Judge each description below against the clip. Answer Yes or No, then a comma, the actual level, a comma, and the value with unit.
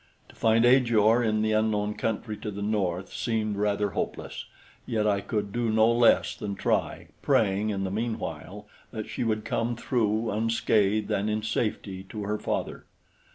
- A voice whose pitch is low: Yes, low, 110 Hz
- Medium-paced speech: Yes, average, 165 wpm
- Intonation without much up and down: Yes, narrow, 1.6 semitones